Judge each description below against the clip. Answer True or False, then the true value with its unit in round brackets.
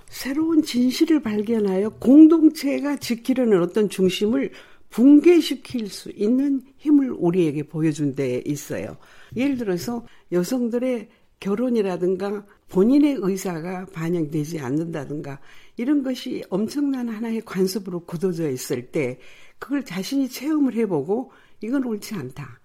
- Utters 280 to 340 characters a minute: True (290 characters per minute)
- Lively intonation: True (7.0 semitones)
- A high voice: True (220 Hz)